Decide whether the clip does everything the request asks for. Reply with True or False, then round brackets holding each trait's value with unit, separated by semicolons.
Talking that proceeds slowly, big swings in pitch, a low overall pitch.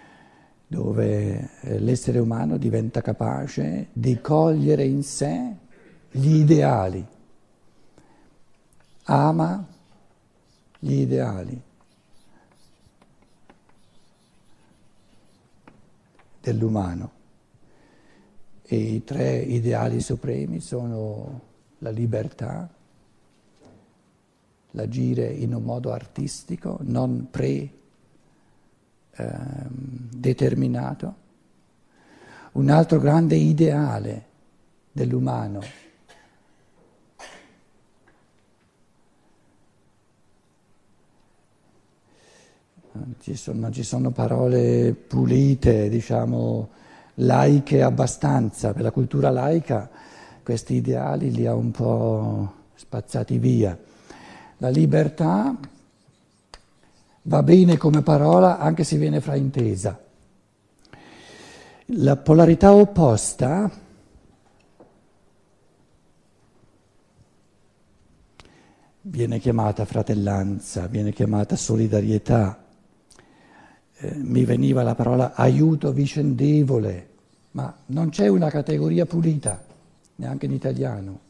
True (70 wpm; 5.9 semitones; 120 Hz)